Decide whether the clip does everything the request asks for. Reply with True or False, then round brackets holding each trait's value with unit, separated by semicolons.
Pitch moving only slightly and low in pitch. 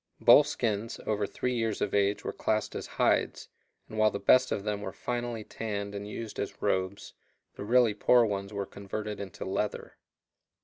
True (2.2 semitones; 105 Hz)